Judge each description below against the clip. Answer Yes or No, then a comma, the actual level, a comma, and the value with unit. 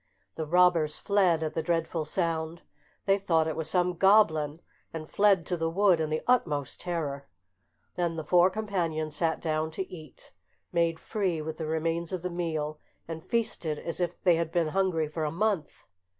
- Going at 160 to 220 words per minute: Yes, average, 180 wpm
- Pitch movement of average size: No, narrow, 2.3 semitones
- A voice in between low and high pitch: Yes, medium, 165 Hz